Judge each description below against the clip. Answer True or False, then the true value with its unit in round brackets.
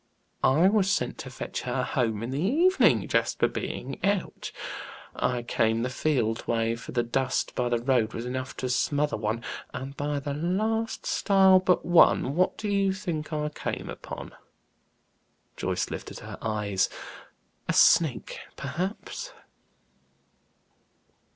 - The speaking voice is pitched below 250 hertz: True (140 Hz)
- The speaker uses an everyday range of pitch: False (7.7 semitones)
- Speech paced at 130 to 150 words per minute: True (140 wpm)